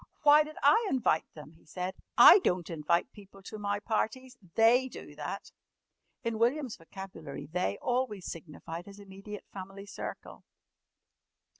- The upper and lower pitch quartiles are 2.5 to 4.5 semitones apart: No, wide, 5.5 semitones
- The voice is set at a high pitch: Yes, high, 200 Hz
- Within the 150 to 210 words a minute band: No, average, 140 wpm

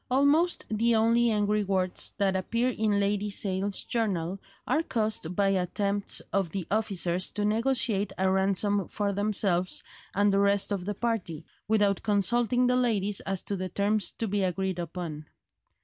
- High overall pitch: Yes, high, 200 Hz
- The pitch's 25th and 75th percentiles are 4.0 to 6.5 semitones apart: No, narrow, 2.5 semitones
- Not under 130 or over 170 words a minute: Yes, average, 160 wpm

